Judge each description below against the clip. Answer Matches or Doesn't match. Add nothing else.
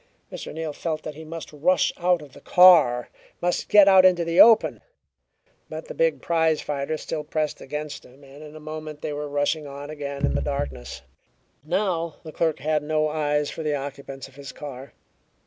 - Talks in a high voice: Doesn't match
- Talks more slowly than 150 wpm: Doesn't match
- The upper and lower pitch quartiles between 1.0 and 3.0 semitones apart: Matches